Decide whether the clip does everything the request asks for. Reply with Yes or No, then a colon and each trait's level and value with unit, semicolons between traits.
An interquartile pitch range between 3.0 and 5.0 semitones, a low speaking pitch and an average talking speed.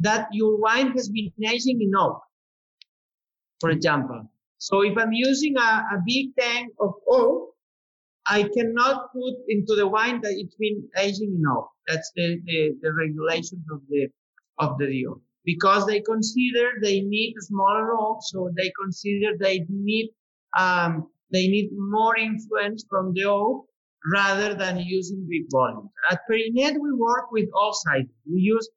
No: average, 3.9 semitones; high, 205 Hz; average, 155 wpm